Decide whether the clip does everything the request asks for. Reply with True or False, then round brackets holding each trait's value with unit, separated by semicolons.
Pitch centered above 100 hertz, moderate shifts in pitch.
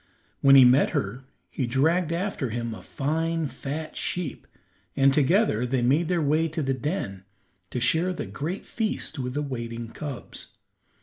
True (140 Hz; 4.6 semitones)